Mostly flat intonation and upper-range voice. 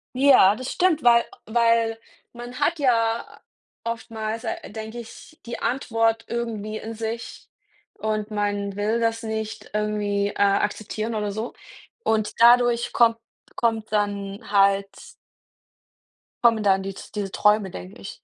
Yes: narrow, 2.1 semitones; high, 220 Hz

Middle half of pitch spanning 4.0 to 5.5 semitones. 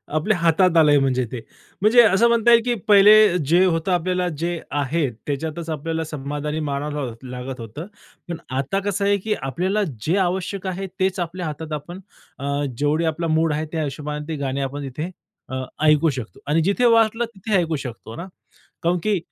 Yes: average, 4.4 semitones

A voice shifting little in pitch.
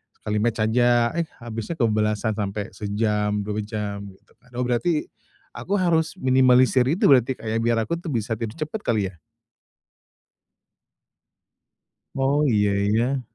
No: average, 3.9 semitones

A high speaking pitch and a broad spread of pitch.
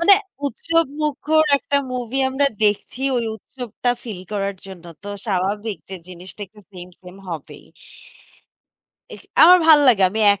Yes: high, 220 Hz; wide, 6.6 semitones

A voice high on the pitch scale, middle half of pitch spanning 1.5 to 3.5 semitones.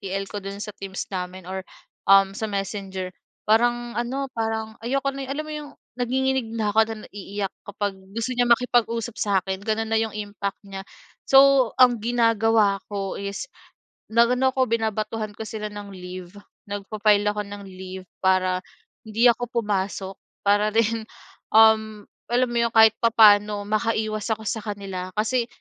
Yes: high, 215 Hz; average, 2.8 semitones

